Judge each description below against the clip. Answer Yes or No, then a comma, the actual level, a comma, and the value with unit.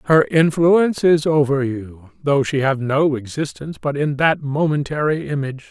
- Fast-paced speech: No, average, 160 wpm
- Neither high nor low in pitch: Yes, medium, 145 Hz